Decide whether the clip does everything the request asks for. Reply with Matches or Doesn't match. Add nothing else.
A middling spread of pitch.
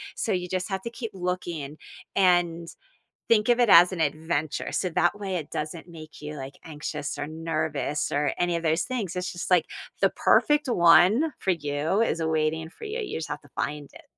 Matches